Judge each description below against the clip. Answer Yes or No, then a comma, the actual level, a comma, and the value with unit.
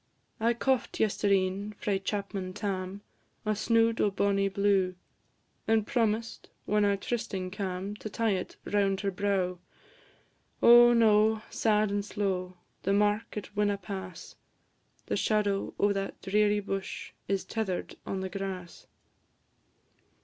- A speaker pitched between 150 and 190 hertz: No, high, 200 Hz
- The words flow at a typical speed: No, slow, 130 wpm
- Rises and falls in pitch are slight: Yes, narrow, 1.7 semitones